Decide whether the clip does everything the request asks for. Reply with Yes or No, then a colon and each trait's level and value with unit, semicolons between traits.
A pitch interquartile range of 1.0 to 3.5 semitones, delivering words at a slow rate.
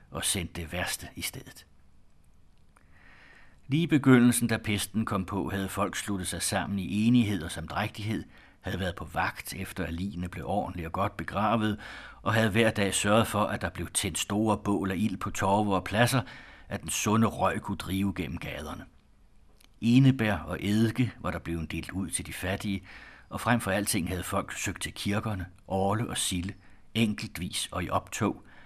No: average, 3.2 semitones; average, 180 wpm